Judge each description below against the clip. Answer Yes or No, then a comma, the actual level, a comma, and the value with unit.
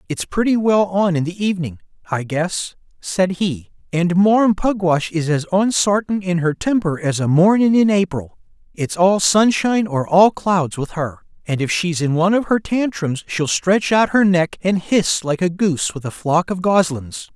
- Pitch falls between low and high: Yes, medium, 180 Hz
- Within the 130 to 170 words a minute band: No, average, 195 wpm